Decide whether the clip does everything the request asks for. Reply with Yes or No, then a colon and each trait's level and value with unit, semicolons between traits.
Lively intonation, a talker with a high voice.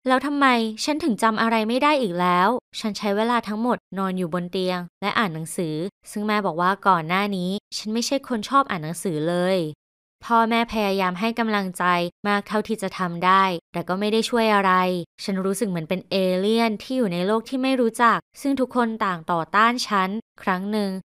No: average, 3.9 semitones; high, 205 Hz